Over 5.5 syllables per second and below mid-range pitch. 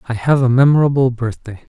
Yes: 6.0 syllables/s; low, 125 Hz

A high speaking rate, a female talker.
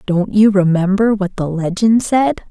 No: average, 170 wpm; female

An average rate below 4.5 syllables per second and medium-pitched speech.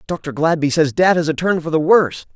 No: 5.6 syllables/s; medium, 160 Hz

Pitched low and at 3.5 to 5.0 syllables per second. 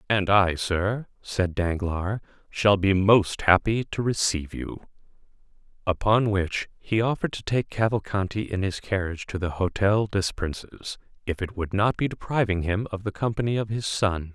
Yes: low, 100 Hz; 4.7 syllables/s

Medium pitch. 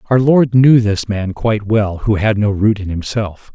No: low, 105 Hz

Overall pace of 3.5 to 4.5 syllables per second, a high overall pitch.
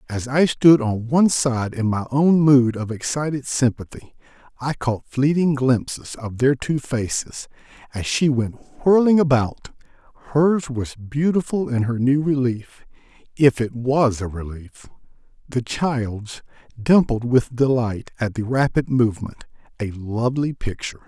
No: 4.3 syllables/s; low, 130 Hz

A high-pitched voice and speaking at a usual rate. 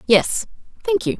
Yes: very high, 270 Hz; average, 150 wpm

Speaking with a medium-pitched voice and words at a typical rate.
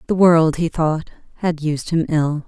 Yes: medium, 160 Hz; average, 195 wpm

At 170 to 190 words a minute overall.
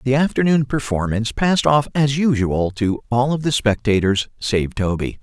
No: average, 160 wpm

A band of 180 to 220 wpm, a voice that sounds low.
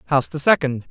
No: average, 200 wpm; medium, 145 Hz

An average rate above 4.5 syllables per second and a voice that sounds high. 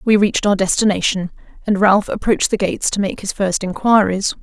Yes: 5.9 syllables/s; high, 200 Hz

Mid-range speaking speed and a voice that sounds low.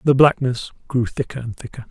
Yes: average, 190 wpm; low, 125 Hz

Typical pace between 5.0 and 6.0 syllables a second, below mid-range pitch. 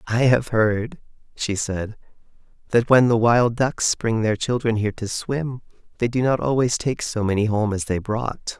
No: 4.4 syllables/s; low, 115 Hz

